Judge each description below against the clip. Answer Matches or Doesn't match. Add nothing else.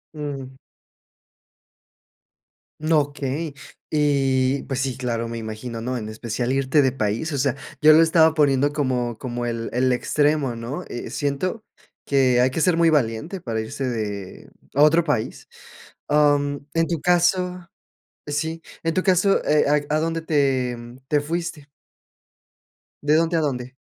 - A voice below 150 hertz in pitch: Matches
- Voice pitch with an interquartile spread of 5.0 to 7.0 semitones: Doesn't match